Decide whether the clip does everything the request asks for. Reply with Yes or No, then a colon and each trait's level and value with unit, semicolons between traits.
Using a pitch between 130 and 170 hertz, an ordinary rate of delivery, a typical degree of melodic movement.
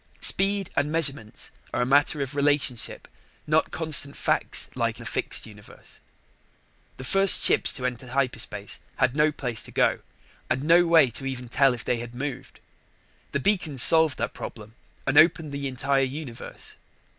Yes: medium, 140 Hz; average, 160 wpm; average, 3.6 semitones